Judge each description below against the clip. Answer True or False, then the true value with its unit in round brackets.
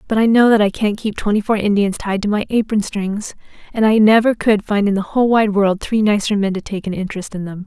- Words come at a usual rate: False (265 wpm)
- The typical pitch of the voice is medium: False (205 Hz)